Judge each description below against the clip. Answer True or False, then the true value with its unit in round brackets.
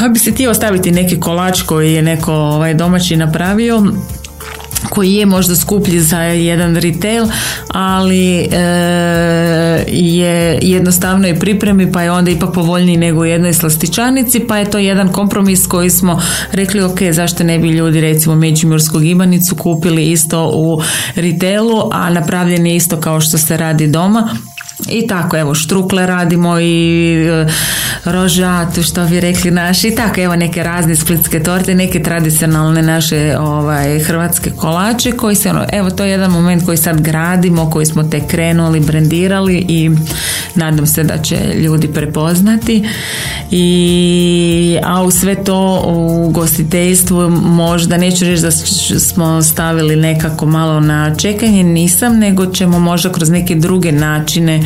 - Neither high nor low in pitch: True (175 Hz)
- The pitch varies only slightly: True (2.2 semitones)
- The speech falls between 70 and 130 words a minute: False (150 wpm)